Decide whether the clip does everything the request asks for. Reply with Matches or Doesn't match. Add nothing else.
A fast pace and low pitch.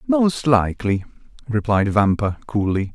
Doesn't match